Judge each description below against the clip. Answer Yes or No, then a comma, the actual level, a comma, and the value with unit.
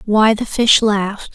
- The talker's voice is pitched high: Yes, high, 215 Hz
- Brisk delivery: No, average, 180 wpm